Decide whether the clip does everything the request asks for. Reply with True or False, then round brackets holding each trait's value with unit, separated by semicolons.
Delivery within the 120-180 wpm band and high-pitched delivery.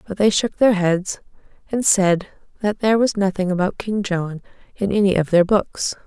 False (190 wpm; 195 Hz)